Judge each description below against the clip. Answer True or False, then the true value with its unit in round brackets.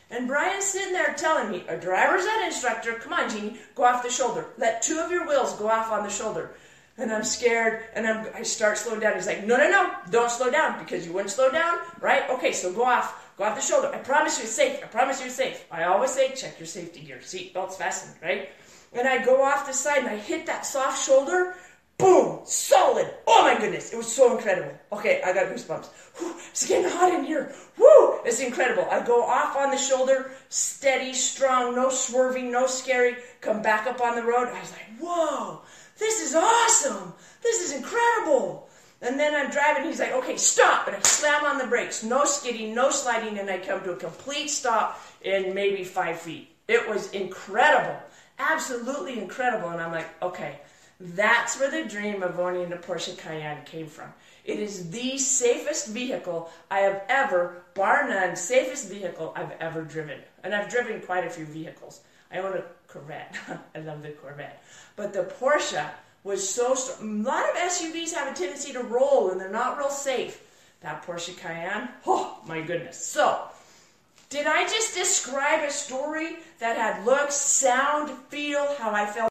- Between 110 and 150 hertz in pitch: False (245 Hz)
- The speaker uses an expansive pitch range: True (7.0 semitones)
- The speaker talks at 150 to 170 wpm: False (195 wpm)